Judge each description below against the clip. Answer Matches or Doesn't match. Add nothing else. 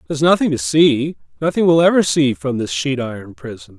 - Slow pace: Doesn't match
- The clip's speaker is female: Doesn't match